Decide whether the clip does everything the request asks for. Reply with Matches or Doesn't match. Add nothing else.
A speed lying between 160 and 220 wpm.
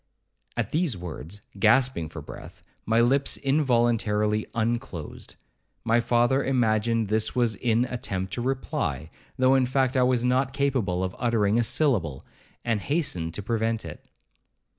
Doesn't match